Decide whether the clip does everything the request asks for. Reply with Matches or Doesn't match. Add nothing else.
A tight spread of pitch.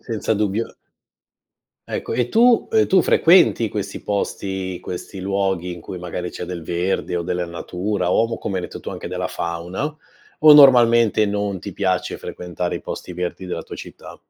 Doesn't match